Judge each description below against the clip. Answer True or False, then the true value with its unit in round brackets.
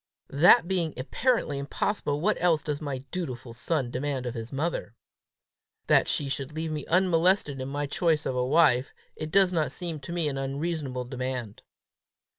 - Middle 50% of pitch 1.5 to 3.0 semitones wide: False (4.3 semitones)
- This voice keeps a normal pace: True (170 wpm)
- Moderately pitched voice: True (145 Hz)